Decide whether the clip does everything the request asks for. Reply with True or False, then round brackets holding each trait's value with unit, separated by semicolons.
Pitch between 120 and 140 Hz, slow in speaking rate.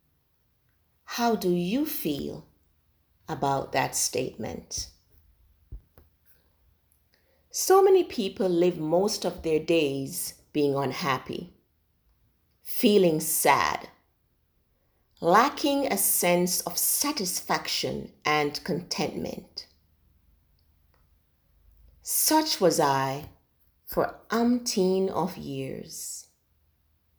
True (135 Hz; 75 wpm)